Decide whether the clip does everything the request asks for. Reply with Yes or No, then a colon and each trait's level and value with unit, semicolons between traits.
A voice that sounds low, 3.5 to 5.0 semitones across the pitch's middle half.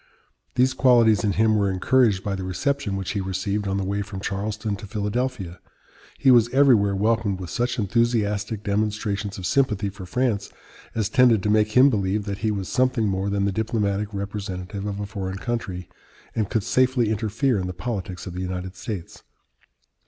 No: low, 105 Hz; average, 2.9 semitones